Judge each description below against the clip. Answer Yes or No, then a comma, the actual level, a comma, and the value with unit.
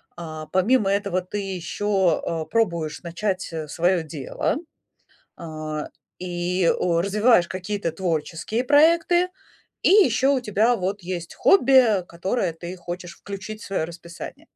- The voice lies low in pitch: No, medium, 185 Hz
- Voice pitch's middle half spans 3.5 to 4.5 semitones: Yes, average, 3.9 semitones